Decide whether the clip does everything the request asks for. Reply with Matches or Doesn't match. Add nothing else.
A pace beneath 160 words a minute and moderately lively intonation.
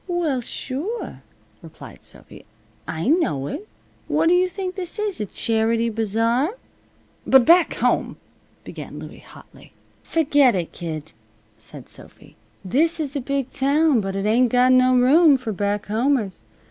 Doesn't match